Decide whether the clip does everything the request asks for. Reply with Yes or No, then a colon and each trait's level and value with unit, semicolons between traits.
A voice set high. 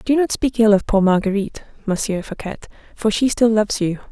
Yes: high, 215 Hz